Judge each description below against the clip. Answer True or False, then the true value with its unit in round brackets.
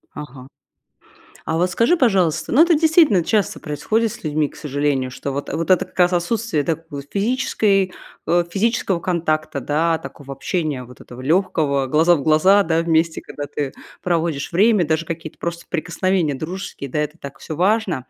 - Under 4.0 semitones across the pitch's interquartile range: False (4.4 semitones)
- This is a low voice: False (165 Hz)